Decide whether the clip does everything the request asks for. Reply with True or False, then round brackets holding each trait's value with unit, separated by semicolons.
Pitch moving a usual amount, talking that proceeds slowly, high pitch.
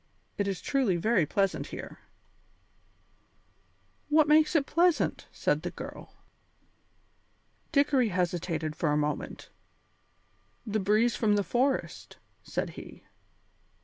False (7.6 semitones; 110 wpm; 210 Hz)